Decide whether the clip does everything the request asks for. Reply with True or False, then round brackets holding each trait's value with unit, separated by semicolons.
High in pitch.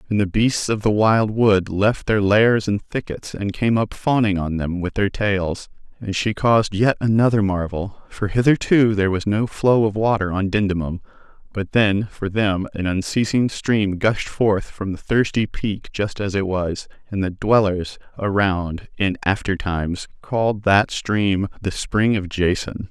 False (100 Hz)